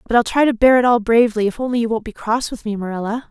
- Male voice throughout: No, female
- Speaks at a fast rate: Yes, fast, 310 wpm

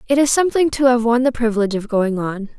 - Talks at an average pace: No, fast, 255 wpm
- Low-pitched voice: No, high, 240 Hz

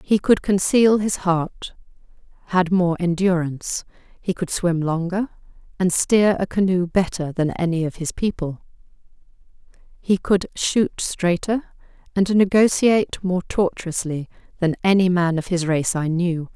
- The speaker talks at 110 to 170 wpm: Yes, average, 140 wpm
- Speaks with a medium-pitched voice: Yes, medium, 180 Hz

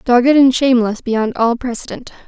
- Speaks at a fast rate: No, average, 160 wpm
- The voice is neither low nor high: No, high, 245 Hz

